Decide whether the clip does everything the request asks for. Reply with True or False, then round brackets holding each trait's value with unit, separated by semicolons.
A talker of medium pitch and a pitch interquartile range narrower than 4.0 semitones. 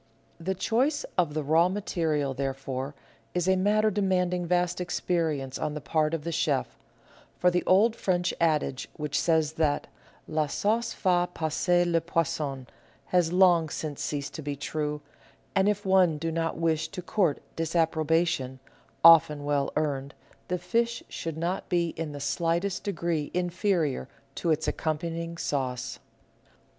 True (165 Hz; 3.2 semitones)